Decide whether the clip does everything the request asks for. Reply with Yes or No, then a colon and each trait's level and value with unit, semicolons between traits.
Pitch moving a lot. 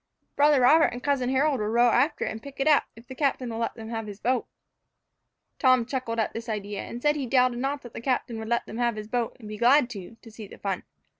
No: average, 2.9 semitones